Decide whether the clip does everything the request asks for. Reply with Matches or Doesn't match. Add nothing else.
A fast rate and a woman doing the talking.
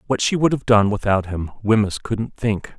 Doesn't match